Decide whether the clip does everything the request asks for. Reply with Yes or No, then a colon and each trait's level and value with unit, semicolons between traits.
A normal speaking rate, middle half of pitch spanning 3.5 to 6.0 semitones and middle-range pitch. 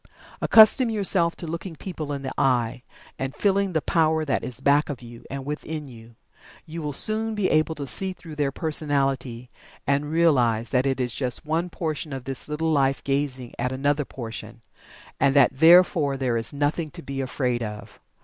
Yes: average, 185 wpm; average, 3.8 semitones; medium, 145 Hz